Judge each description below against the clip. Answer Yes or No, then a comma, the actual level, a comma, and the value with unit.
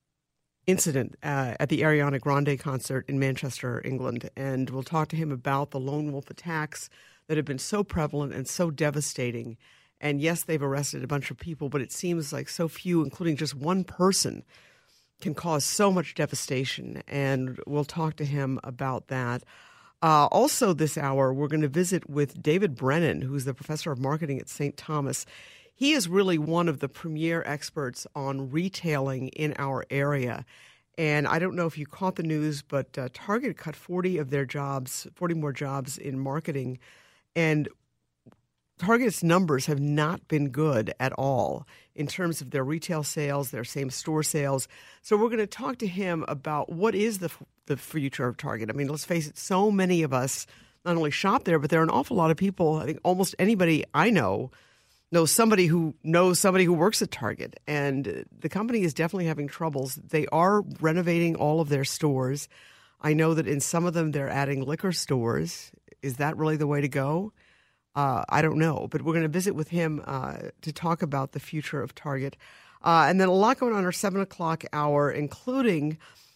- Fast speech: No, average, 195 wpm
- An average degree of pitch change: Yes, average, 3.6 semitones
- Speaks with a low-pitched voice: No, medium, 150 Hz